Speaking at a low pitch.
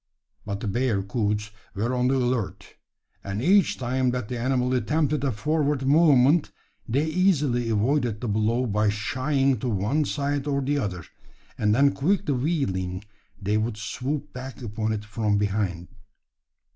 Yes: low, 125 Hz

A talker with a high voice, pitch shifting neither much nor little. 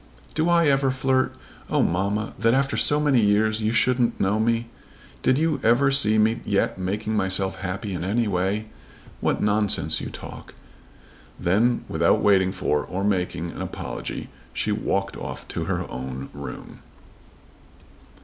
No: low, 105 Hz; average, 4.1 semitones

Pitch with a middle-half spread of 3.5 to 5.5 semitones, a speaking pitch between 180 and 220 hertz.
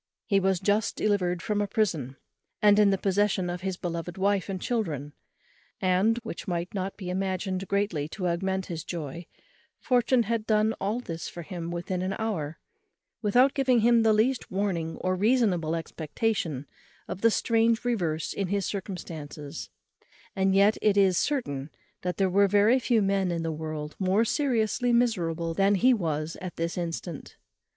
Yes: average, 4.1 semitones; high, 190 Hz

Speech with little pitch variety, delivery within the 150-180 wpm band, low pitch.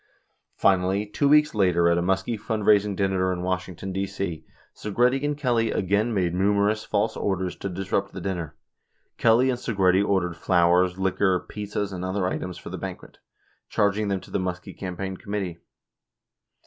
Yes: narrow, 2.3 semitones; average, 165 wpm; very low, 95 Hz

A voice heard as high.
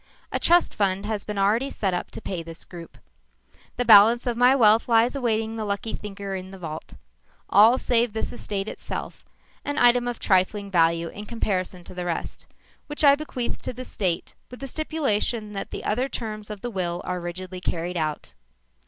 Yes: high, 210 Hz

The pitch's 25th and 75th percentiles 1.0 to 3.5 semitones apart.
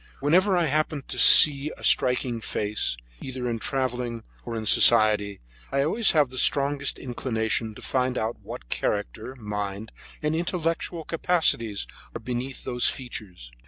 No: average, 4.7 semitones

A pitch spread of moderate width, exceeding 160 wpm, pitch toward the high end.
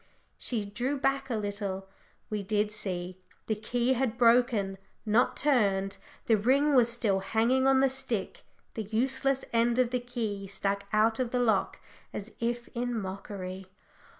No: average, 3.7 semitones; average, 155 wpm; high, 225 Hz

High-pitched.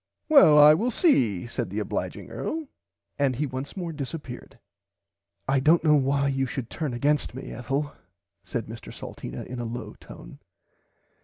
No: medium, 140 Hz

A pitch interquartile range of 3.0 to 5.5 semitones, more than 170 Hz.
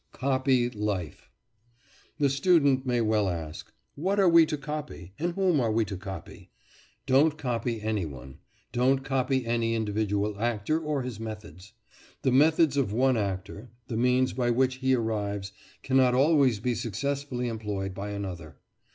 No: average, 4.6 semitones; low, 120 Hz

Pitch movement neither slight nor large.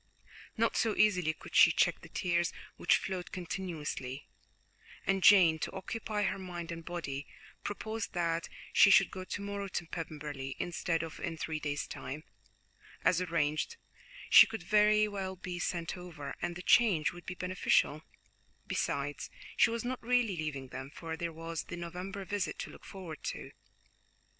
Yes: average, 3.5 semitones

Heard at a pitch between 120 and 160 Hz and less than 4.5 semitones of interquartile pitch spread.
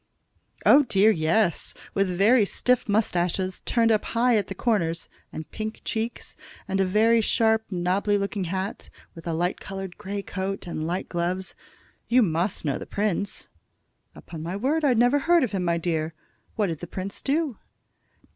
No: high, 195 Hz; average, 4.1 semitones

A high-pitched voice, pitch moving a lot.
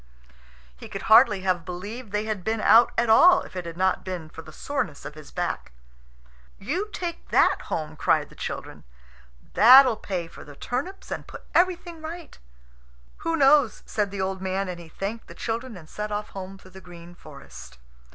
Yes: high, 200 Hz; wide, 6.0 semitones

